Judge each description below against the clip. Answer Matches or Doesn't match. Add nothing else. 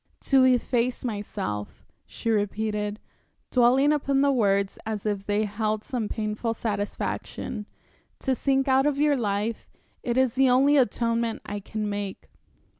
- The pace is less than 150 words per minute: Matches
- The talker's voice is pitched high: Matches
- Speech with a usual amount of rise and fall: Matches